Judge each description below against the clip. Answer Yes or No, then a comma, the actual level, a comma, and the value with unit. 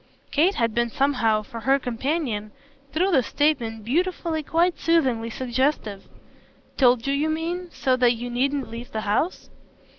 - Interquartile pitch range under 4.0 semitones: No, average, 5.3 semitones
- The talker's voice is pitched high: Yes, very high, 260 Hz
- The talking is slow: No, average, 150 wpm